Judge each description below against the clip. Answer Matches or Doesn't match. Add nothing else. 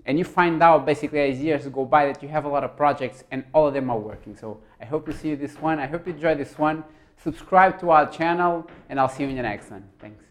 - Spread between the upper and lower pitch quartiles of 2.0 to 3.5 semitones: Matches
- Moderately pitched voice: Matches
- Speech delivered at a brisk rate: Matches